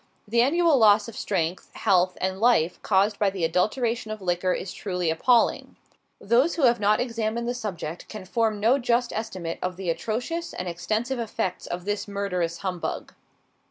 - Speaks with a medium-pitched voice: No, high, 210 Hz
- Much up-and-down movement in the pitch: No, average, 4.4 semitones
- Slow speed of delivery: No, average, 170 wpm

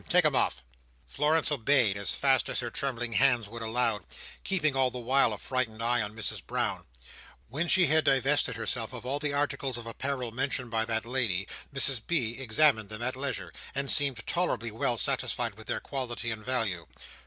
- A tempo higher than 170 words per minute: Yes, average, 190 wpm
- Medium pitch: No, low, 125 Hz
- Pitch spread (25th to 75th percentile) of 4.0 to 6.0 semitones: No, average, 3.4 semitones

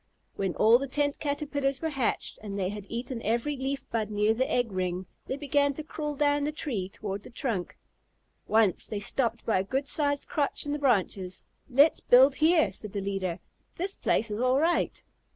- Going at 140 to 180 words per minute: No, average, 195 wpm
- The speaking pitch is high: Yes, very high, 250 Hz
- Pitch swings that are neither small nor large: No, wide, 5.8 semitones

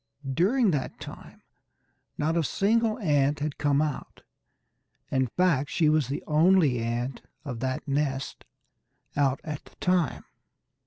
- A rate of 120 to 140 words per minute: Yes, slow, 135 wpm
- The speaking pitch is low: No, medium, 150 Hz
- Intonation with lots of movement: No, average, 4.1 semitones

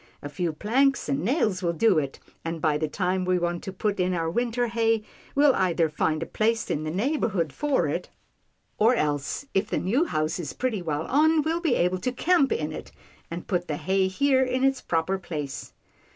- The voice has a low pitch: No, high, 190 Hz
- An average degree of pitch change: No, wide, 7.2 semitones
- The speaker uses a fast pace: Yes, fast, 210 wpm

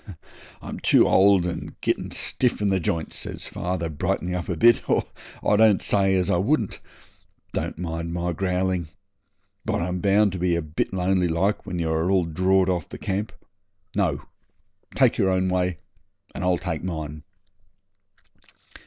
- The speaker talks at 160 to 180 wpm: Yes, average, 165 wpm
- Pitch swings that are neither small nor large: No, narrow, 2.1 semitones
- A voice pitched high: No, very low, 90 Hz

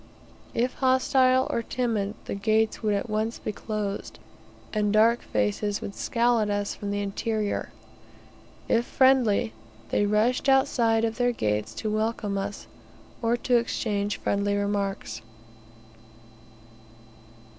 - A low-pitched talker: No, high, 215 Hz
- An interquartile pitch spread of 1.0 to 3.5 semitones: Yes, narrow, 2.6 semitones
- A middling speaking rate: No, slow, 125 wpm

